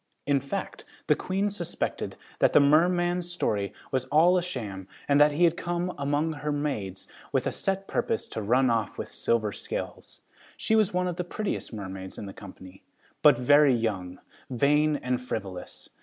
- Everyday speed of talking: Yes, average, 175 wpm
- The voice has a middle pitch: Yes, medium, 145 Hz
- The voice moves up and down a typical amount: No, wide, 8.0 semitones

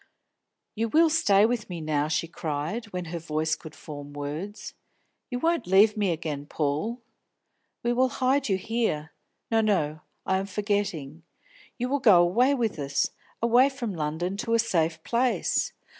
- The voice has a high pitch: Yes, high, 195 Hz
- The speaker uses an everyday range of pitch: No, wide, 6.8 semitones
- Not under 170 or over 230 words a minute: No, average, 160 wpm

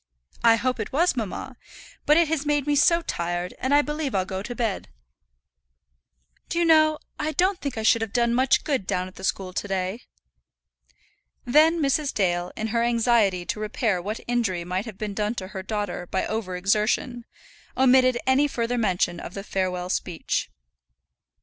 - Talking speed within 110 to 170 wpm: No, average, 180 wpm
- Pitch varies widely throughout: Yes, wide, 5.9 semitones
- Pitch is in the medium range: No, high, 225 Hz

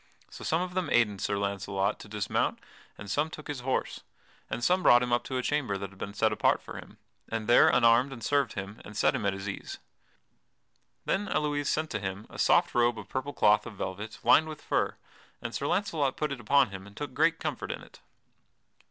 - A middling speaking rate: No, fast, 220 wpm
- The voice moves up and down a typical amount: No, wide, 6.1 semitones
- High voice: No, low, 120 Hz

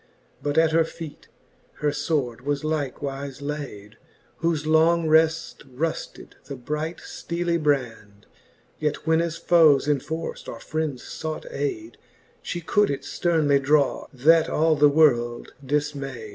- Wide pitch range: No, average, 2.7 semitones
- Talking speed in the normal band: No, slow, 130 wpm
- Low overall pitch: No, medium, 150 Hz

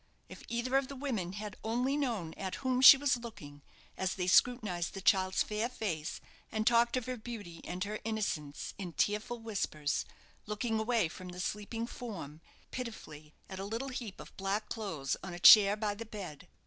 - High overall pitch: Yes, high, 210 Hz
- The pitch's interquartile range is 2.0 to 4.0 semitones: No, average, 4.5 semitones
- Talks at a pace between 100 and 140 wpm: No, average, 185 wpm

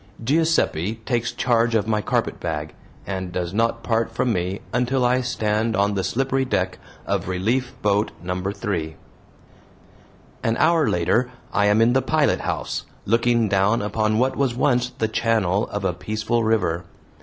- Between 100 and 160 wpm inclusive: Yes, average, 155 wpm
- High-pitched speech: No, low, 110 Hz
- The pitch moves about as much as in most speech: Yes, average, 4.0 semitones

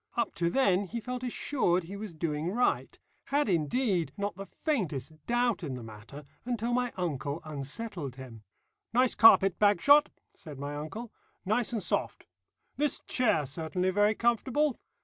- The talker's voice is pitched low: No, high, 195 Hz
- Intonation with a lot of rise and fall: Yes, wide, 7.6 semitones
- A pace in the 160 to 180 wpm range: No, average, 150 wpm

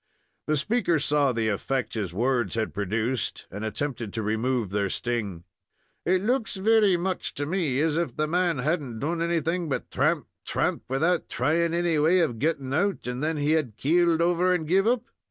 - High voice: No, medium, 150 Hz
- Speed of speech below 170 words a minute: No, average, 185 wpm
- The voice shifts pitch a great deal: Yes, wide, 6.1 semitones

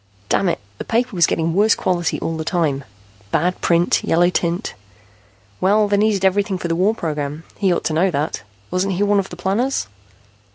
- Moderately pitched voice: Yes, medium, 180 Hz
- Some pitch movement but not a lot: Yes, average, 3.3 semitones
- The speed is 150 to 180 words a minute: No, average, 195 wpm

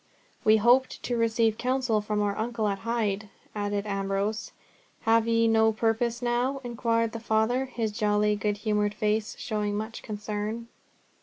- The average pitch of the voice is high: Yes, high, 220 Hz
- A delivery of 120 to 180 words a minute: Yes, average, 150 wpm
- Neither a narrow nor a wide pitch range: No, narrow, 1.8 semitones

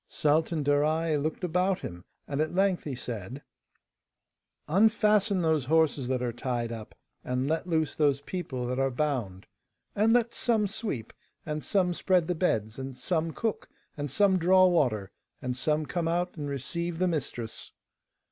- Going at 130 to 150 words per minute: No, average, 160 wpm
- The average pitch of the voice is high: No, medium, 155 Hz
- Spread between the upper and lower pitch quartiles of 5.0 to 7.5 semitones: Yes, wide, 5.6 semitones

